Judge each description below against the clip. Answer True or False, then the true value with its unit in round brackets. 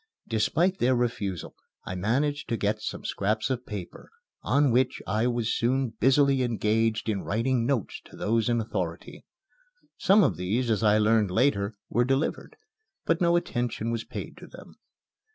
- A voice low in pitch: True (115 Hz)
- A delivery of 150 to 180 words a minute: True (160 wpm)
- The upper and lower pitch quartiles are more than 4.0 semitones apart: False (3.5 semitones)